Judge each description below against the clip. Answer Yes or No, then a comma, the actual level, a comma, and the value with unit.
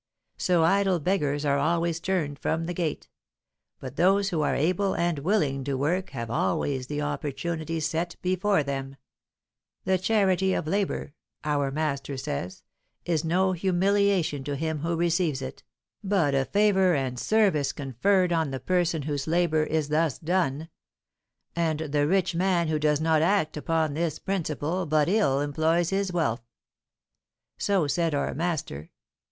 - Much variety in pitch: No, average, 4.0 semitones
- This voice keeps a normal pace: Yes, average, 150 wpm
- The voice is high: No, medium, 160 Hz